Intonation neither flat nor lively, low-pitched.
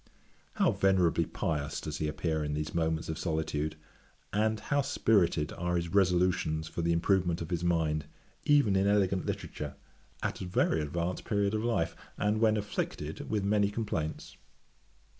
Yes: average, 4.2 semitones; very low, 85 Hz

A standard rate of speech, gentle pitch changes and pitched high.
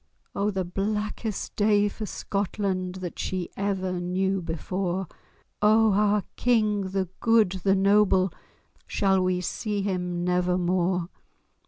No: slow, 120 wpm; narrow, 2.2 semitones; high, 195 Hz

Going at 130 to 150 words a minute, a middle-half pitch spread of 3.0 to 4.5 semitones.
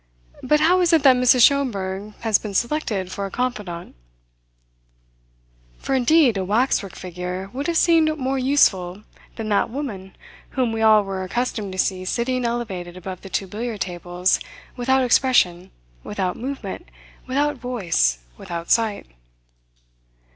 No: average, 140 wpm; wide, 5.5 semitones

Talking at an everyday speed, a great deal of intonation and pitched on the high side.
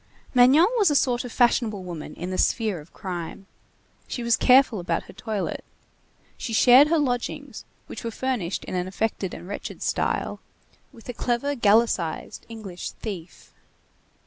No: average, 155 wpm; average, 5.0 semitones; high, 225 Hz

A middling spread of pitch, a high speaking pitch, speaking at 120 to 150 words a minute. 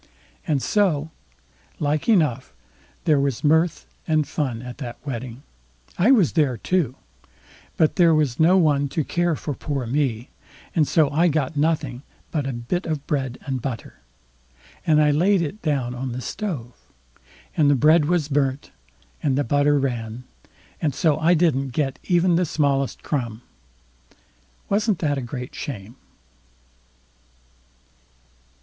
No: average, 3.7 semitones; medium, 145 Hz; average, 145 wpm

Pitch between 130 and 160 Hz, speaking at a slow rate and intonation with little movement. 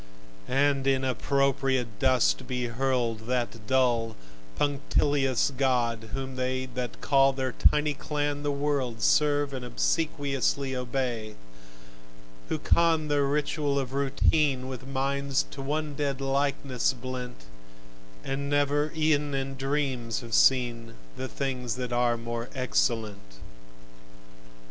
Yes: low, 135 Hz; slow, 120 wpm; narrow, 2.3 semitones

